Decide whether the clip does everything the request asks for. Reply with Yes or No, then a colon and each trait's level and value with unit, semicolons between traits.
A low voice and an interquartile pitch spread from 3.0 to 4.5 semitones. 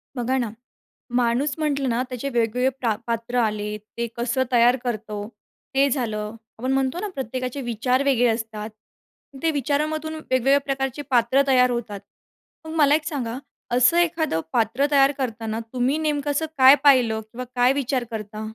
No: very high, 250 Hz; average, 3.3 semitones